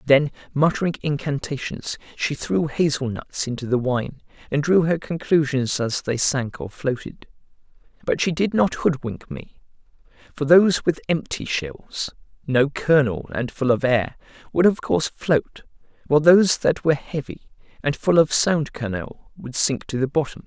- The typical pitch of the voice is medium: Yes, medium, 145 Hz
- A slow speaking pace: No, average, 160 wpm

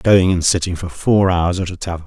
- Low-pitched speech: Yes, very low, 90 Hz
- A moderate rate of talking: No, fast, 260 wpm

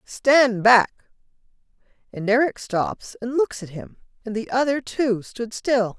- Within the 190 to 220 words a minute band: No, average, 150 wpm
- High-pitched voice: Yes, high, 235 Hz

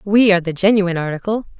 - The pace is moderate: Yes, average, 190 wpm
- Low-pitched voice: No, high, 190 Hz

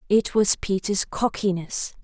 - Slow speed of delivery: Yes, slow, 120 wpm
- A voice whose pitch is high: Yes, high, 195 Hz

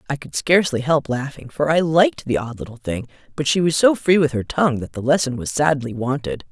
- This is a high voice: No, medium, 140 Hz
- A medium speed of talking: No, fast, 240 wpm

